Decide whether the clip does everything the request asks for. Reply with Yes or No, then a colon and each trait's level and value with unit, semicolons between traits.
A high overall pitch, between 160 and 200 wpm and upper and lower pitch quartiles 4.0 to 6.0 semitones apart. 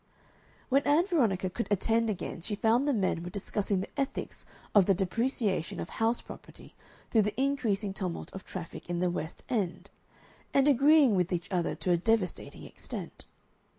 Yes: high, 205 Hz; average, 170 wpm; average, 5.2 semitones